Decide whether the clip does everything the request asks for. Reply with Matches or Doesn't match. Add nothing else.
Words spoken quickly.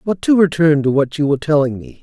Matches